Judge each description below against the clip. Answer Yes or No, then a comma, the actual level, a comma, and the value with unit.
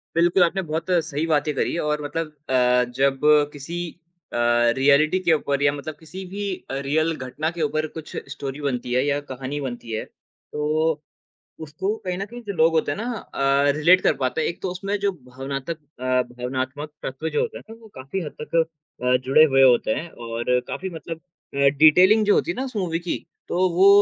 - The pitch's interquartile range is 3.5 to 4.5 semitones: Yes, average, 4.2 semitones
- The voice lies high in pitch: No, medium, 150 Hz